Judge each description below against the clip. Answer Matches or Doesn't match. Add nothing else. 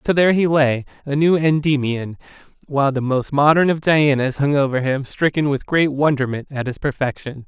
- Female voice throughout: Doesn't match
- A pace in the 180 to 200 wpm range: Matches